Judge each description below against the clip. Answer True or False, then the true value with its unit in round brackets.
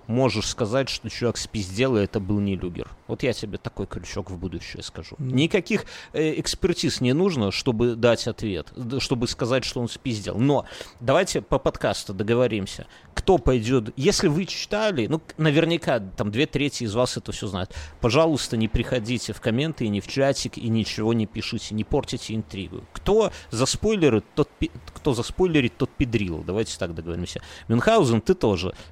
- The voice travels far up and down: False (4.5 semitones)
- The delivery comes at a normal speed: False (170 wpm)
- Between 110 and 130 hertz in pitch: True (115 Hz)